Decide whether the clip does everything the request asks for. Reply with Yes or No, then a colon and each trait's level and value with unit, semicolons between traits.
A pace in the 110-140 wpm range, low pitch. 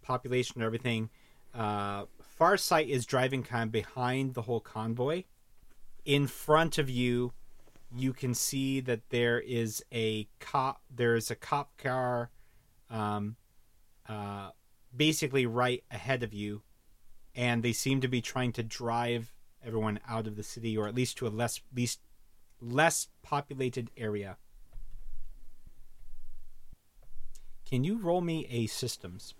Yes: slow, 135 wpm; low, 120 Hz